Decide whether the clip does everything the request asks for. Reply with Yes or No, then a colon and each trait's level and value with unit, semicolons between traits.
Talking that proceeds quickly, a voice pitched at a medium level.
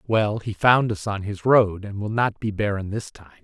No: fast, 245 wpm; low, 105 Hz